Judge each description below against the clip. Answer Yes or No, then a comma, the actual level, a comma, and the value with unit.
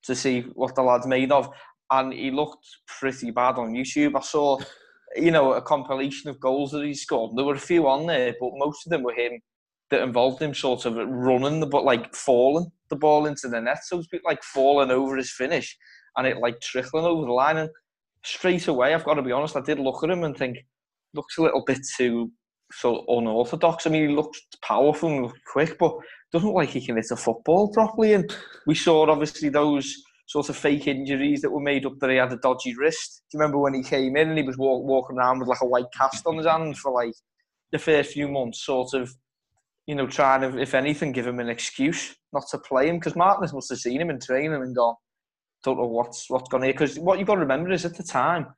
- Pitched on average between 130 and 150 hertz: Yes, medium, 140 Hz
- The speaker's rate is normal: No, fast, 245 wpm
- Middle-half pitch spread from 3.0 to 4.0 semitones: Yes, average, 3.4 semitones